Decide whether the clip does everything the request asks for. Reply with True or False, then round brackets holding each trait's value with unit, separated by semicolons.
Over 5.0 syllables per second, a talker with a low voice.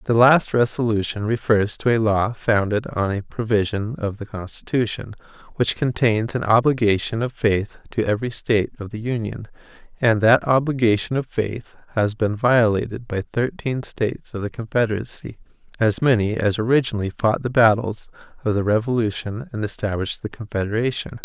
True (5.2 syllables/s; 110 Hz)